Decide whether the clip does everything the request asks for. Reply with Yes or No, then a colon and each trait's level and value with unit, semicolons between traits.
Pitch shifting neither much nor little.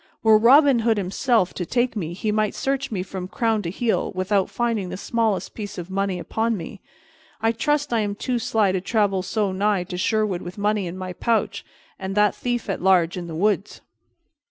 Yes: average, 3.2 semitones